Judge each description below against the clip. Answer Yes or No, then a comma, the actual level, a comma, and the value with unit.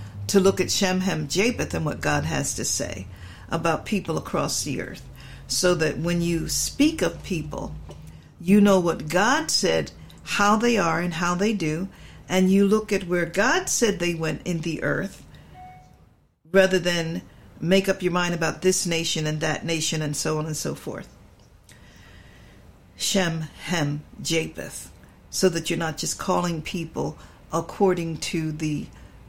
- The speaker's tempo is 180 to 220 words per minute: No, average, 160 wpm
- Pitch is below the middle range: No, medium, 170 Hz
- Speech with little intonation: No, average, 3.3 semitones